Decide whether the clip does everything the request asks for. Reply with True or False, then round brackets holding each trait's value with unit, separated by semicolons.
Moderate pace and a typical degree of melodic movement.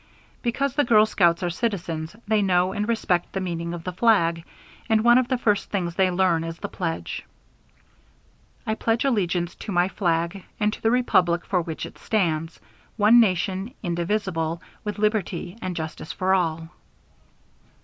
True (165 wpm; 4.1 semitones)